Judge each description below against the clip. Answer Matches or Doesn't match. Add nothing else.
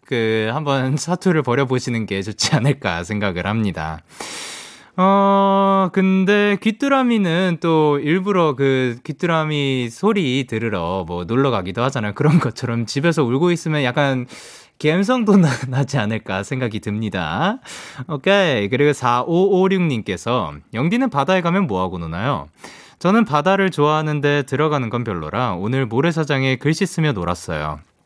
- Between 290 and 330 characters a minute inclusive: Matches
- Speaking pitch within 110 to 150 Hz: Matches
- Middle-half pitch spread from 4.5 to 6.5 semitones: Doesn't match